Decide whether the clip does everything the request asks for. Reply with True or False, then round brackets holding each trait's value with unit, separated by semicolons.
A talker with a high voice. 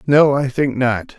False (130 Hz)